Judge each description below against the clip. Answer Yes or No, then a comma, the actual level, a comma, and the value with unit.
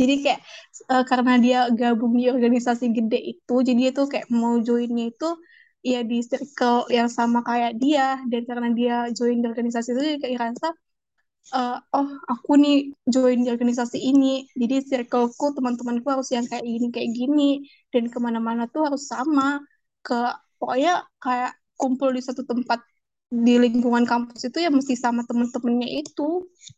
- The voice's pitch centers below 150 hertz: No, very high, 250 Hz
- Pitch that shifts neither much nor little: No, narrow, 2.2 semitones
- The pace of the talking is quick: Yes, fast, 160 wpm